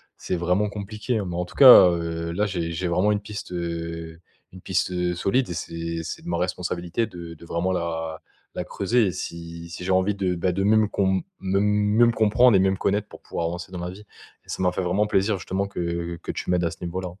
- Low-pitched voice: Yes, very low, 90 Hz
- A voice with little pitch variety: No, average, 3.1 semitones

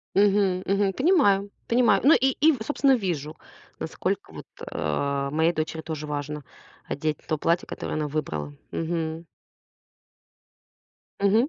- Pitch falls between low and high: Yes, medium, 170 Hz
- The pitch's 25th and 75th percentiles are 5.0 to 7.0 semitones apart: Yes, average, 5.3 semitones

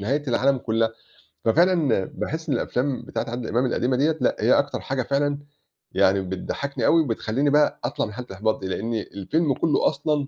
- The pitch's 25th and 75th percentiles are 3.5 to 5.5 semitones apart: Yes, average, 4.4 semitones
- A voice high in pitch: No, low, 130 Hz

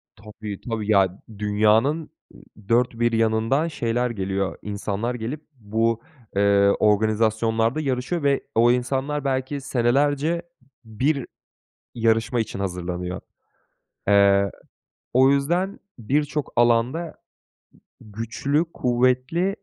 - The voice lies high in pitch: No, low, 115 Hz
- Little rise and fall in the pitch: No, average, 4.3 semitones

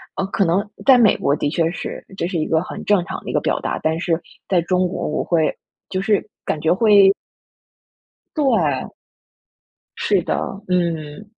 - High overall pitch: No, medium, 180 Hz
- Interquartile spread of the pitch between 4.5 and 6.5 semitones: No, average, 3.7 semitones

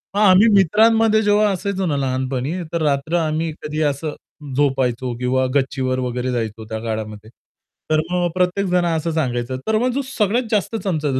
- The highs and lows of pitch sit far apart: Yes, wide, 7.1 semitones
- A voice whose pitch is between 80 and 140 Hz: No, medium, 155 Hz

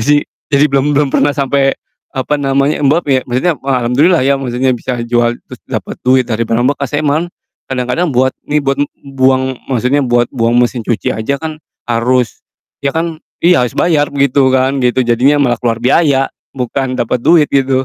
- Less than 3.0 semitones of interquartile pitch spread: Yes, narrow, 2.5 semitones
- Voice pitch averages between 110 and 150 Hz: Yes, low, 135 Hz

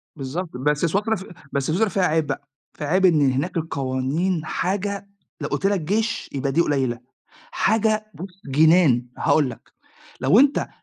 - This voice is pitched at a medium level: Yes, medium, 165 Hz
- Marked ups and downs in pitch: Yes, wide, 5.7 semitones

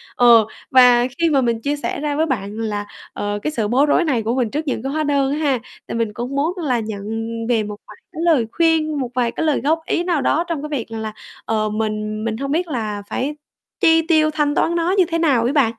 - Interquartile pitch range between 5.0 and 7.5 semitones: Yes, wide, 5.5 semitones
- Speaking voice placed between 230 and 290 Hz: Yes, very high, 270 Hz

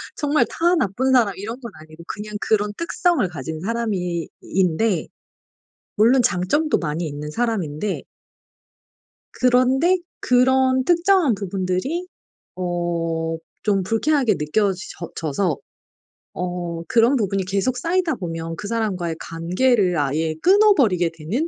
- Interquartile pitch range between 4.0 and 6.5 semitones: No, wide, 7.1 semitones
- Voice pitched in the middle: No, high, 200 Hz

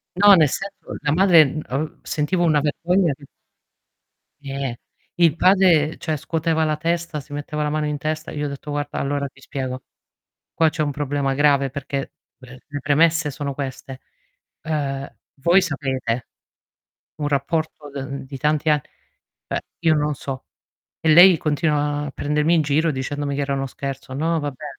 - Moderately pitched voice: Yes, medium, 150 Hz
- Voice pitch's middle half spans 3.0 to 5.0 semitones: No, narrow, 2.4 semitones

